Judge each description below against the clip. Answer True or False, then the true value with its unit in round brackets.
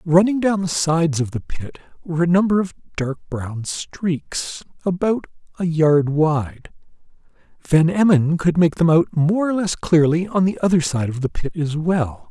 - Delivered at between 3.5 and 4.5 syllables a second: True (4.4 syllables/s)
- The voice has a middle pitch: True (165 Hz)